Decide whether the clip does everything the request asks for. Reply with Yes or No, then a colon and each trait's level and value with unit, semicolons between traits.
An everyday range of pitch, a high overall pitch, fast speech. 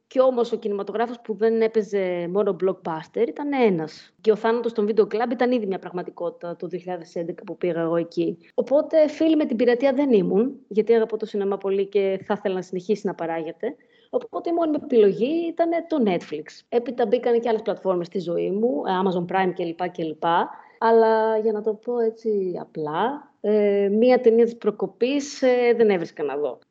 Yes: average, 4.6 semitones; high, 220 Hz; fast, 185 wpm